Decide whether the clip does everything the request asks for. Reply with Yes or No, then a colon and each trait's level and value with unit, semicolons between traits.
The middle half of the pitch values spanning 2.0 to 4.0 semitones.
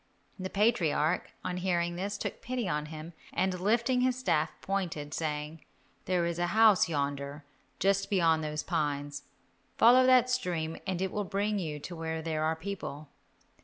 No: average, 4.4 semitones